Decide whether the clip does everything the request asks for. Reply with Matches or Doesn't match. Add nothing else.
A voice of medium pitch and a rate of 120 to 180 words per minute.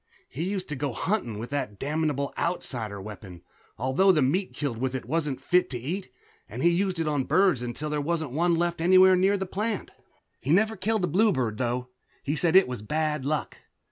Doesn't match